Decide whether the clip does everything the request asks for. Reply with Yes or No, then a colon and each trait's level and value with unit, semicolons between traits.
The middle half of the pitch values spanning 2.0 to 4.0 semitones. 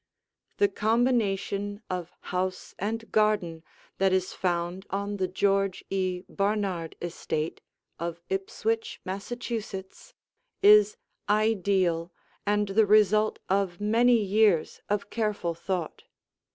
Yes: average, 2.8 semitones